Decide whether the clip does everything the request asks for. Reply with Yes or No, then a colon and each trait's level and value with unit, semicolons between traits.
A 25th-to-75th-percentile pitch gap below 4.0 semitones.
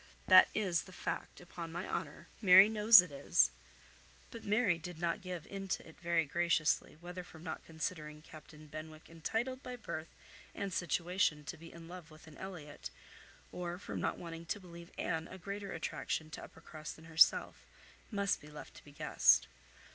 Yes: average, 3.0 semitones